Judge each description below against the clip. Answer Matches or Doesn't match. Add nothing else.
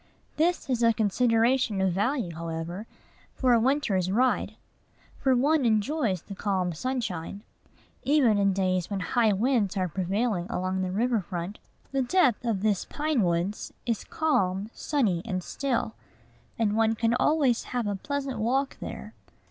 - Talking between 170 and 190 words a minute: Doesn't match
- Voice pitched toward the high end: Matches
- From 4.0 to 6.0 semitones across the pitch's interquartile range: Matches